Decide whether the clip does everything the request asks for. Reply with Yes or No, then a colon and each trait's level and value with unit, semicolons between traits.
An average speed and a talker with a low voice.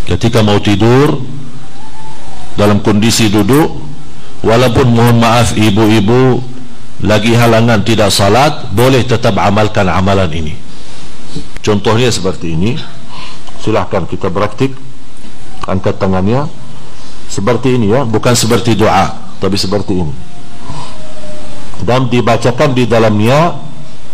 Yes: average, 100 wpm; low, 115 Hz